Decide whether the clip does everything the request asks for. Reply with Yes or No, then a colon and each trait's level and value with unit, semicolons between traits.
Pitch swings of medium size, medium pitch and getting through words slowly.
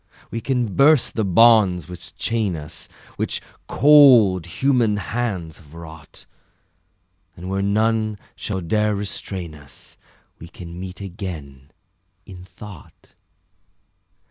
No: average, 4.7 semitones; very low, 95 Hz; slow, 115 wpm